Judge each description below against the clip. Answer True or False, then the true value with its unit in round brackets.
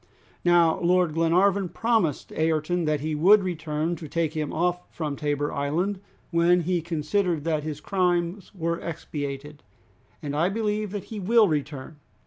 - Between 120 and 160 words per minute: True (150 wpm)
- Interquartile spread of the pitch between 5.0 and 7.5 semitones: False (3.1 semitones)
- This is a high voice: False (170 Hz)